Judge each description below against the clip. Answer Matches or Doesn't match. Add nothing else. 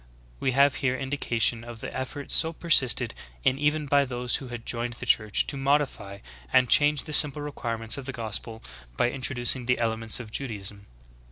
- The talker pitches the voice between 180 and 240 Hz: Doesn't match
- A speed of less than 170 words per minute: Doesn't match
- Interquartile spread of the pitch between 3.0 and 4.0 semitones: Matches